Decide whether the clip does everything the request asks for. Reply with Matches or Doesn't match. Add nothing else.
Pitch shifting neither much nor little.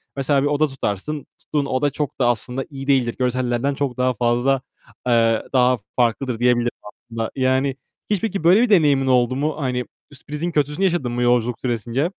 Matches